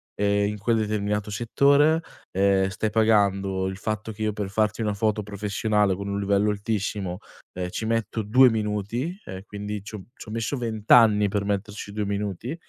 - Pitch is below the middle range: Yes, low, 105 Hz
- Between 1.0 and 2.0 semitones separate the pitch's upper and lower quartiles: Yes, narrow, 1.6 semitones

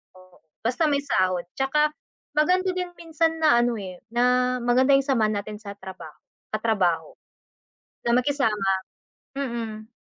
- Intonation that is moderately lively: No, wide, 5.7 semitones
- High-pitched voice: Yes, high, 240 Hz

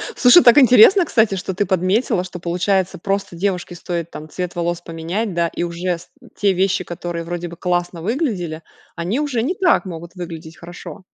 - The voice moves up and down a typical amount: Yes, average, 3.0 semitones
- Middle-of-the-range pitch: Yes, medium, 180 Hz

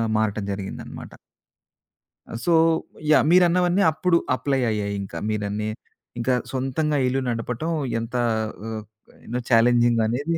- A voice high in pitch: No, low, 120 Hz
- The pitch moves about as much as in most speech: No, wide, 5.8 semitones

